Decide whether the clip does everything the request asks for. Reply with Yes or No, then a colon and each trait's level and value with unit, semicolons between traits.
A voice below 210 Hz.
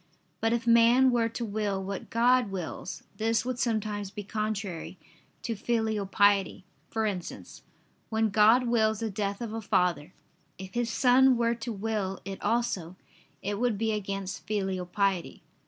No: high, 215 Hz